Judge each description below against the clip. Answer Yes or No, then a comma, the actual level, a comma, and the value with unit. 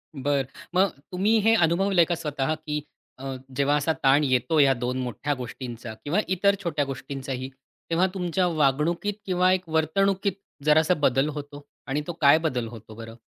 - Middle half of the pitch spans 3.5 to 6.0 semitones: Yes, average, 4.8 semitones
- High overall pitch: No, medium, 150 Hz